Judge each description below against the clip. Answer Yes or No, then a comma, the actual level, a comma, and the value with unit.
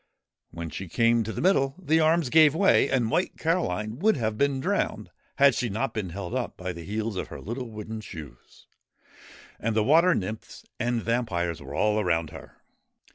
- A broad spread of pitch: Yes, wide, 5.9 semitones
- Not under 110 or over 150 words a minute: No, average, 185 wpm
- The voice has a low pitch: Yes, low, 115 Hz